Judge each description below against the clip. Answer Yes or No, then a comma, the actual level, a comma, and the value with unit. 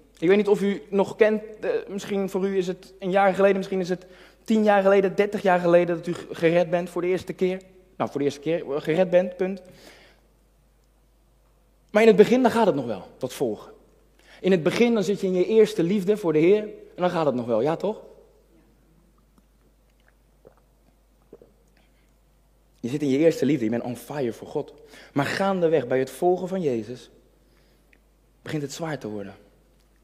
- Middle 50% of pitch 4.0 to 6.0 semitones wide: No, average, 3.5 semitones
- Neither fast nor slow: Yes, average, 190 wpm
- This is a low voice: No, medium, 185 Hz